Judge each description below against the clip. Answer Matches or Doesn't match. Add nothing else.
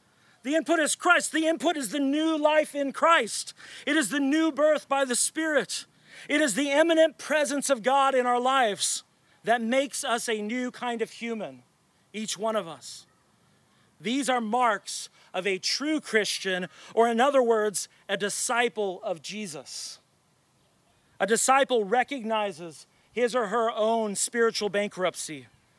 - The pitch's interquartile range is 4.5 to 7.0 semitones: Matches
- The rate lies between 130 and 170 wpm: Matches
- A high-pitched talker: Matches